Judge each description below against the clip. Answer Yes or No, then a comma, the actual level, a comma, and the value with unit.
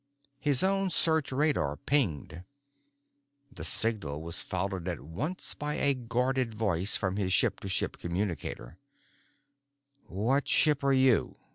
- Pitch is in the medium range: No, low, 115 Hz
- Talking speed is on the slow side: Yes, slow, 130 wpm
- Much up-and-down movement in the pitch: Yes, wide, 7.2 semitones